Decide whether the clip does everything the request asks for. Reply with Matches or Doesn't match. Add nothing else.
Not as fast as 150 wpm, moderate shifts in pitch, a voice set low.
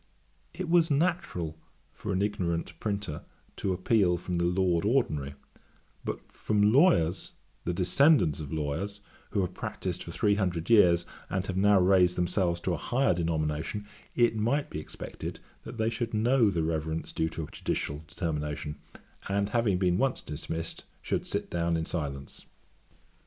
Doesn't match